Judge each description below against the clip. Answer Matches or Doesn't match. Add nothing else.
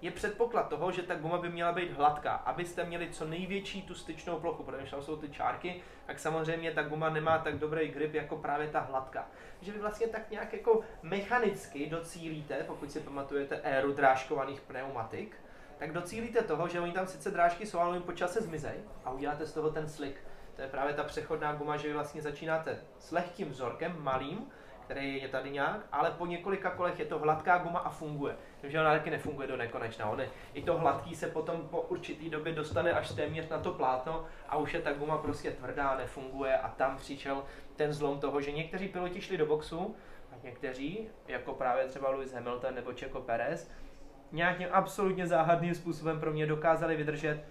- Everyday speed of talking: Doesn't match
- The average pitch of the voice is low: Doesn't match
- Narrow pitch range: Doesn't match